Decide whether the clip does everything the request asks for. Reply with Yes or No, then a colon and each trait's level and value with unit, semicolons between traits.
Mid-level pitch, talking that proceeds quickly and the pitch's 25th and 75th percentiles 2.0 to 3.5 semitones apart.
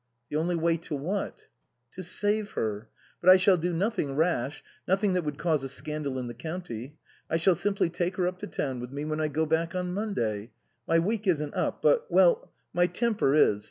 No: medium, 165 Hz; fast, 220 wpm; average, 4.7 semitones